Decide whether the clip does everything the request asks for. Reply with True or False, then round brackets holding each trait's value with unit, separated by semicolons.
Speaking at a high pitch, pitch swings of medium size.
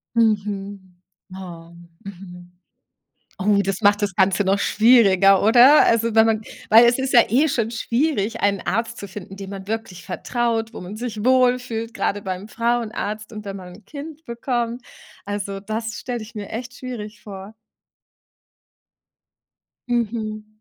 True (215 Hz; 3.1 semitones)